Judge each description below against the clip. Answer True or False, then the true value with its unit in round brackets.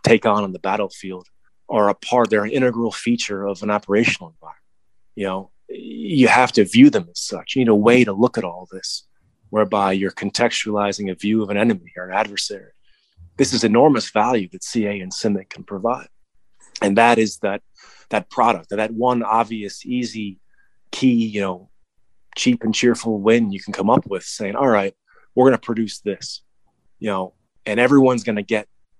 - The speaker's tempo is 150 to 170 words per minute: False (190 wpm)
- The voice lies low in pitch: True (105 Hz)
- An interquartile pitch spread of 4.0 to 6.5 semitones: False (2.9 semitones)